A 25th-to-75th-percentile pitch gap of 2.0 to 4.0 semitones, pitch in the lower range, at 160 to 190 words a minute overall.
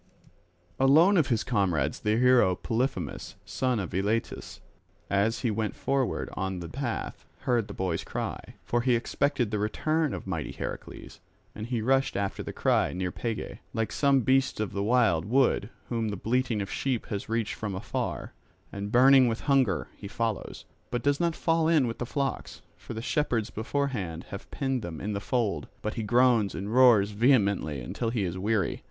No: average, 4.4 semitones; low, 115 Hz; average, 180 wpm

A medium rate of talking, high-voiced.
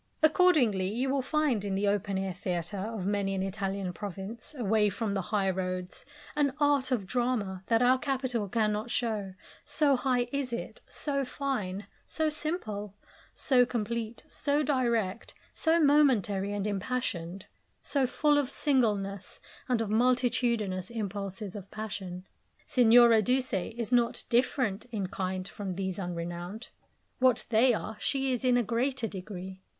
Yes: average, 145 wpm; high, 220 Hz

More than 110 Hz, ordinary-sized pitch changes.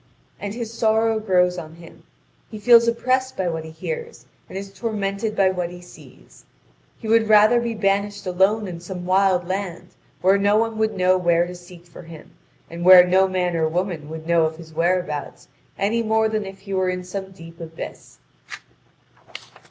Yes: high, 190 Hz; average, 3.6 semitones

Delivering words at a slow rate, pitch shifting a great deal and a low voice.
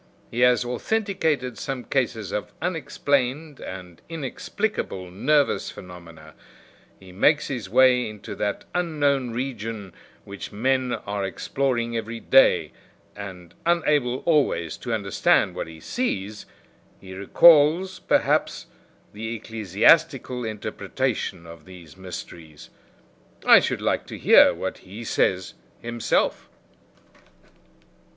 Yes: slow, 110 wpm; wide, 6.3 semitones; low, 115 Hz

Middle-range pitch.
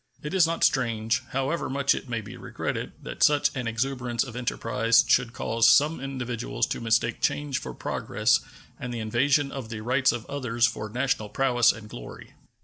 No: low, 120 Hz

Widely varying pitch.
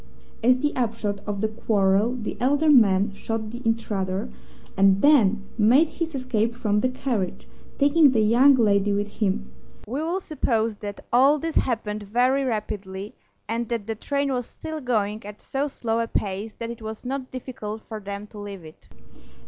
No: average, 3.8 semitones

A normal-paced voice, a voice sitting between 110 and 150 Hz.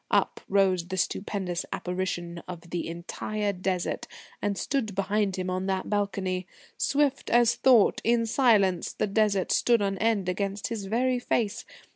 No: average, 150 wpm; high, 200 Hz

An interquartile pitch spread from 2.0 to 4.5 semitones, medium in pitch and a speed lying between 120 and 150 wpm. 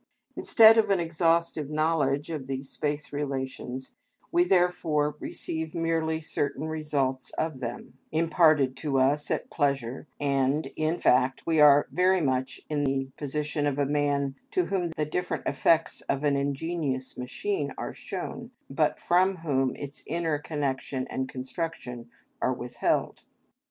Yes: average, 3.5 semitones; medium, 145 Hz; average, 140 wpm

